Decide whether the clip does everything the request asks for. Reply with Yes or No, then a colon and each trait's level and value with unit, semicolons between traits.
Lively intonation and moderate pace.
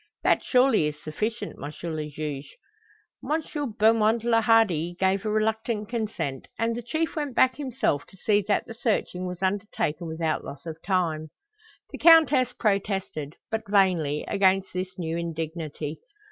Yes: wide, 5.8 semitones; average, 150 wpm